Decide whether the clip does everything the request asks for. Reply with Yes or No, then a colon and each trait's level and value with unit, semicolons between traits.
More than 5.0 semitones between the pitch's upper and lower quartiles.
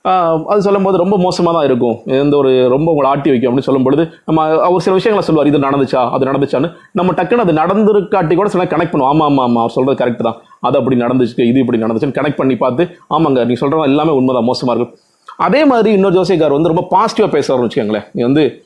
Yes: wide, 5.5 semitones